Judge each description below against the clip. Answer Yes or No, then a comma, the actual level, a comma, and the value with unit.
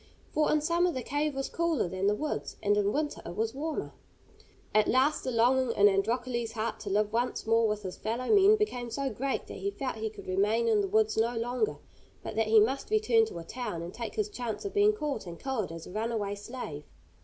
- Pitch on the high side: Yes, high, 235 Hz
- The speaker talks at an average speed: No, fast, 230 wpm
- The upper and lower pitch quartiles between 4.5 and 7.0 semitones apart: Yes, average, 5.1 semitones